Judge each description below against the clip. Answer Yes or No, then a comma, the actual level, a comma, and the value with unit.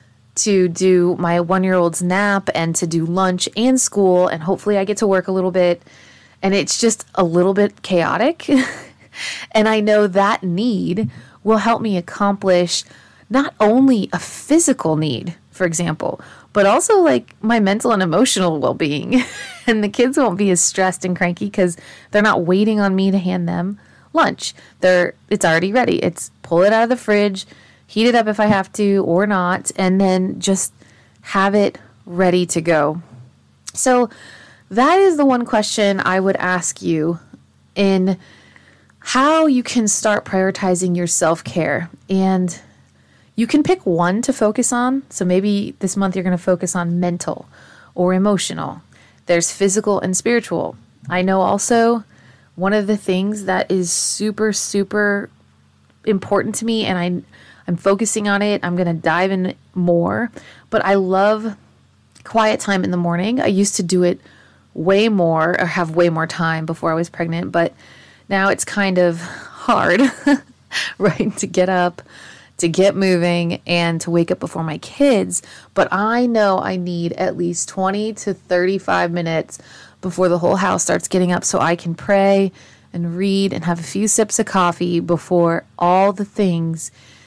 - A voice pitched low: No, high, 190 Hz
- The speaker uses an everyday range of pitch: Yes, average, 3.2 semitones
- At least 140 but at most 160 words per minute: No, average, 170 wpm